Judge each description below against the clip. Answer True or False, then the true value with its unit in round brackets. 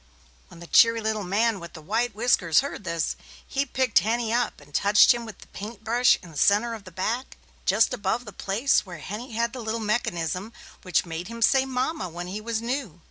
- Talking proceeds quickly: True (215 wpm)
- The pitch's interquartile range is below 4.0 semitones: False (4.3 semitones)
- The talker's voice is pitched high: True (220 Hz)